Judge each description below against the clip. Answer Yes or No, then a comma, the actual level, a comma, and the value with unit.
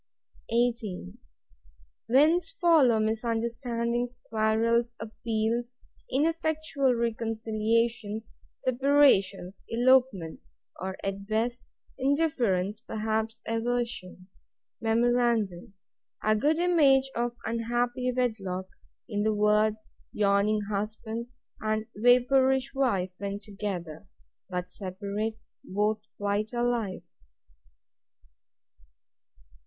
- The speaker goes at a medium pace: No, slow, 75 wpm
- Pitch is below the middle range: No, high, 225 Hz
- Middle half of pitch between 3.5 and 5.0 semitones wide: No, average, 2.8 semitones